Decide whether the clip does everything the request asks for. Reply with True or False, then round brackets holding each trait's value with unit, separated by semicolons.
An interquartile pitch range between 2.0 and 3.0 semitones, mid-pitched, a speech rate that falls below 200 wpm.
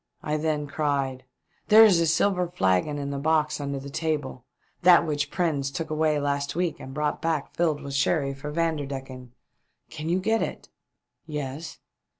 True (2.7 semitones; 150 Hz; 170 wpm)